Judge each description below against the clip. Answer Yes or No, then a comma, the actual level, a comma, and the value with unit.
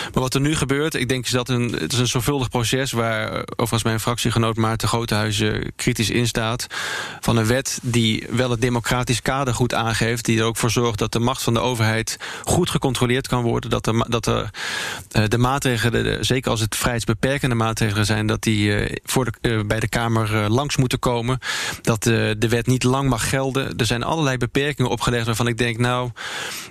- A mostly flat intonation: Yes, narrow, 2.0 semitones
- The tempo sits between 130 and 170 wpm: No, fast, 200 wpm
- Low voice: Yes, low, 120 Hz